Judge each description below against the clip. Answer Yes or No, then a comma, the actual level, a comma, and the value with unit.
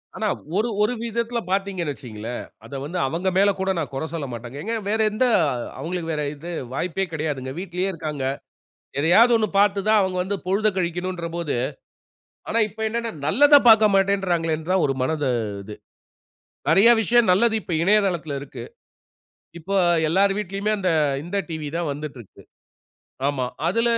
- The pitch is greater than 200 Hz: No, medium, 185 Hz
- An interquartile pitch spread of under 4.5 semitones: No, average, 5.1 semitones